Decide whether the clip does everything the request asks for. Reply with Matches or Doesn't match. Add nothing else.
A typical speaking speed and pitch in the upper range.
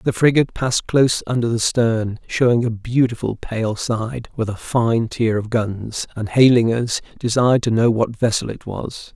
Doesn't match